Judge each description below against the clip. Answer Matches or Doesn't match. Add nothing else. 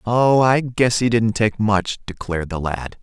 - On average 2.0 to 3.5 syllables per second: Doesn't match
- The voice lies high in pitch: Doesn't match